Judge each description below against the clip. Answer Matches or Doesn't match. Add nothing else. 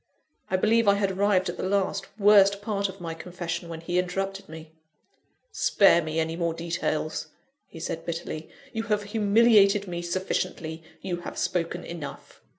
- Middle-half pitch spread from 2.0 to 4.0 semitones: Matches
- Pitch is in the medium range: Matches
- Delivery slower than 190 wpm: Matches